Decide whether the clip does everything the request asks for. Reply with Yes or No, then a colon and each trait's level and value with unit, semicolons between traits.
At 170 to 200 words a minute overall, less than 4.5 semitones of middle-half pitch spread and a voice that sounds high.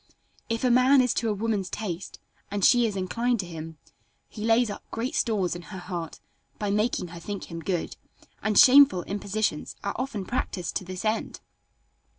Yes: average, 180 wpm; average, 4.1 semitones; high, 205 Hz